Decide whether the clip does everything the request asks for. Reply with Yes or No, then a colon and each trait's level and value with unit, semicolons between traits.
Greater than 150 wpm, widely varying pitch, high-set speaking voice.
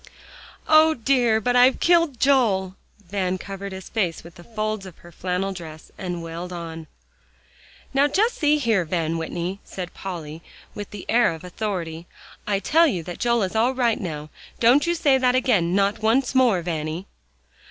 Yes: average, 175 wpm; wide, 6.1 semitones; high, 195 Hz